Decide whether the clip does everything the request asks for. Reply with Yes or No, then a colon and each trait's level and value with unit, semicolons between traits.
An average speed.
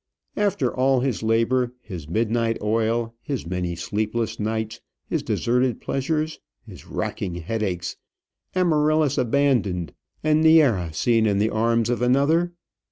No: slow, 125 wpm